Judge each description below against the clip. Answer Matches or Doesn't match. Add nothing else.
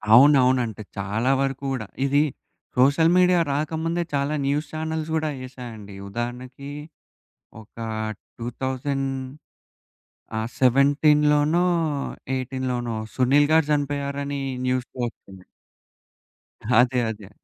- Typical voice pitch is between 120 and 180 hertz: Matches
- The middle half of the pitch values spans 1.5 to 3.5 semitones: Matches